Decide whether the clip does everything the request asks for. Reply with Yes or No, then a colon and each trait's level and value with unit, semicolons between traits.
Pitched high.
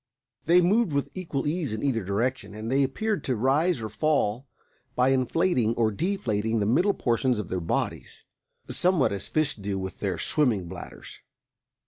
No: low, 130 Hz